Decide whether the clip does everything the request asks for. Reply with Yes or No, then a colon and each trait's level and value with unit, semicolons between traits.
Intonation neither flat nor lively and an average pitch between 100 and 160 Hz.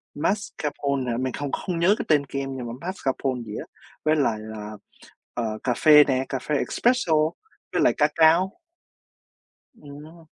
Yes: average, 4.1 semitones; medium, 140 Hz